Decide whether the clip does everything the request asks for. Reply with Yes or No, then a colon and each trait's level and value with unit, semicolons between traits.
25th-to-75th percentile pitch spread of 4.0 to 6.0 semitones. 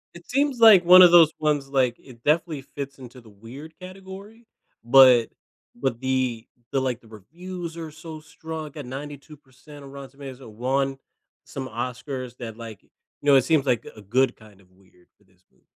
Yes: average, 4.7 semitones